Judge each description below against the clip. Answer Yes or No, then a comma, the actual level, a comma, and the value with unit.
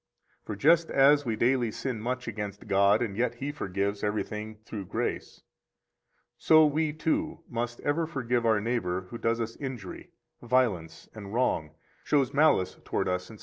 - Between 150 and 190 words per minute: Yes, average, 165 wpm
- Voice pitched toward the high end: No, low, 115 Hz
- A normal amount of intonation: Yes, average, 4.6 semitones